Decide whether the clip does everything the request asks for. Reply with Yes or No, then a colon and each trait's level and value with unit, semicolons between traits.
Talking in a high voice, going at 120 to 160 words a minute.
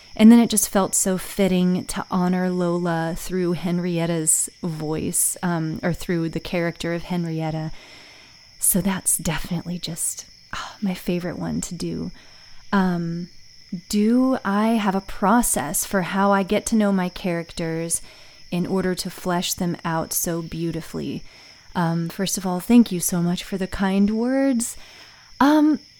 No: medium, 180 Hz; average, 150 wpm